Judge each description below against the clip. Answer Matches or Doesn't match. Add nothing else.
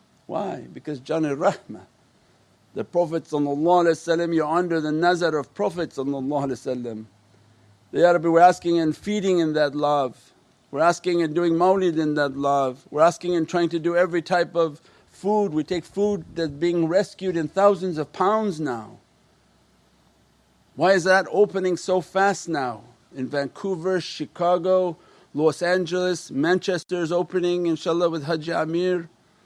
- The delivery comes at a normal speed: Matches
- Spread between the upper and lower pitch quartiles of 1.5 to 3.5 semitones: Matches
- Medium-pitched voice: Matches